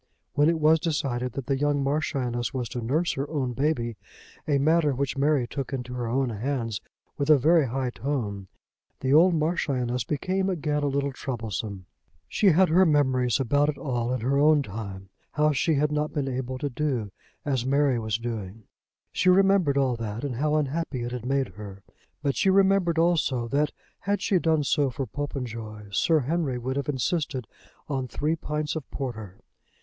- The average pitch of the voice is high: No, medium, 140 Hz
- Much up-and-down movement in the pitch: No, average, 3.8 semitones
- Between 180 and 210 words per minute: Yes, average, 185 wpm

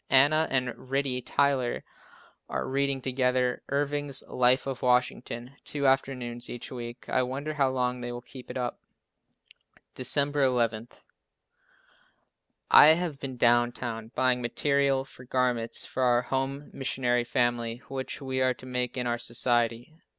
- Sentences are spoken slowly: No, average, 145 wpm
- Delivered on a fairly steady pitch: Yes, narrow, 2.0 semitones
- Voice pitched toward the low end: Yes, low, 125 Hz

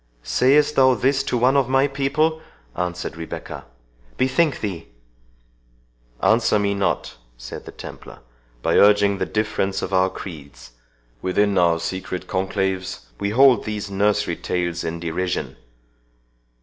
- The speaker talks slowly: Yes, slow, 130 wpm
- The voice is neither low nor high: No, low, 100 Hz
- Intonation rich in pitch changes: Yes, wide, 5.9 semitones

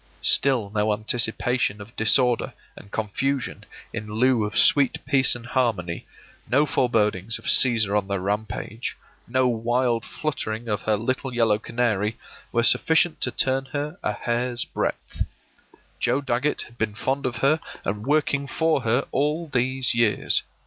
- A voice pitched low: Yes, low, 120 Hz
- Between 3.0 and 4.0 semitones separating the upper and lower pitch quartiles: Yes, average, 3.5 semitones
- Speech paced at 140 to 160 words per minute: Yes, average, 150 wpm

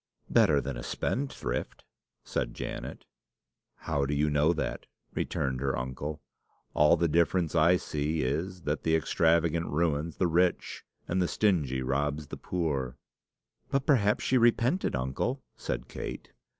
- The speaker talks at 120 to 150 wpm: Yes, average, 140 wpm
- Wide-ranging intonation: No, average, 3.9 semitones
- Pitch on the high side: No, very low, 80 Hz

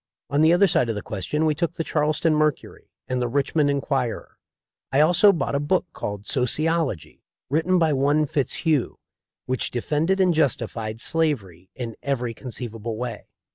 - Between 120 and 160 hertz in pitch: Yes, medium, 140 Hz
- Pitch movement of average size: Yes, average, 4.9 semitones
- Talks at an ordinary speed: Yes, average, 160 wpm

